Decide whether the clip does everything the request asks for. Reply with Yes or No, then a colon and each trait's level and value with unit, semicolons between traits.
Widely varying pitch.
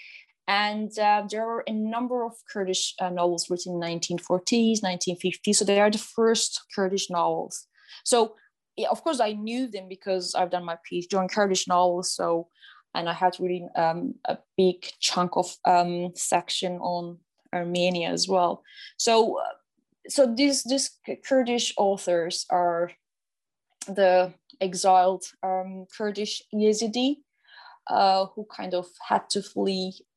No: average, 4.0 semitones